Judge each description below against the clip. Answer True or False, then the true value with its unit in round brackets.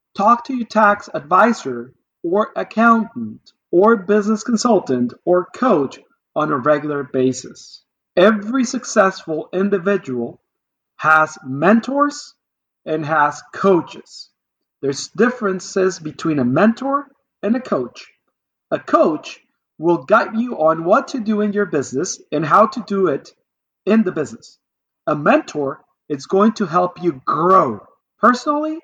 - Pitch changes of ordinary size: False (6.5 semitones)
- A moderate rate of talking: False (125 wpm)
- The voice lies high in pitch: True (195 Hz)